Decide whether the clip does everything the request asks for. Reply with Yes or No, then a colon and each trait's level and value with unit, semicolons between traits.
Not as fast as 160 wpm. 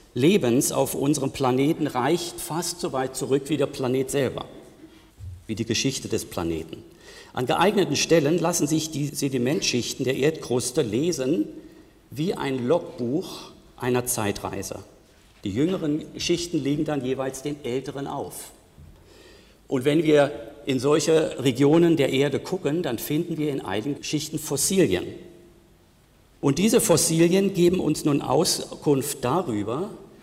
Yes: average, 130 wpm